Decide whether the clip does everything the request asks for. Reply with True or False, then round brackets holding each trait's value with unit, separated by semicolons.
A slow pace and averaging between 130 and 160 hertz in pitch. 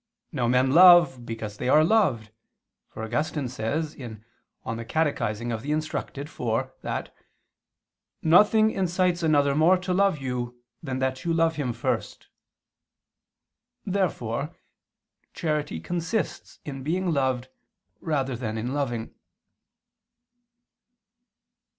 True (105 wpm; 140 Hz)